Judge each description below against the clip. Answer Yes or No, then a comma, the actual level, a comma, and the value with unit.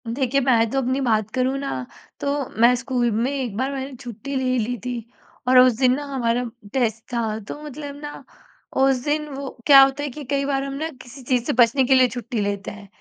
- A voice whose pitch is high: Yes, very high, 255 Hz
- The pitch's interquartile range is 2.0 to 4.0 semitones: Yes, average, 2.7 semitones